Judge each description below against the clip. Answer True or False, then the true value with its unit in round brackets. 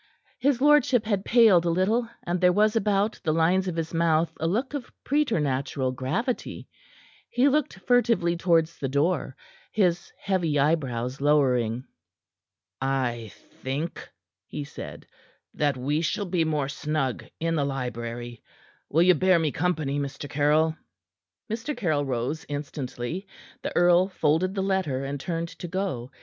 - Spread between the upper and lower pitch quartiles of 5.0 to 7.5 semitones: True (5.4 semitones)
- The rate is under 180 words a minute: True (145 wpm)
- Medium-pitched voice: True (165 Hz)